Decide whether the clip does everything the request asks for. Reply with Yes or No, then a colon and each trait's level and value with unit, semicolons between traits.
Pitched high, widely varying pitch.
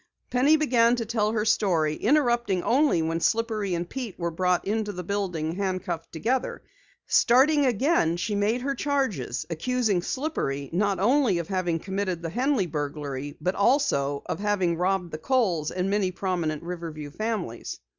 Yes: high, 195 Hz; wide, 5.9 semitones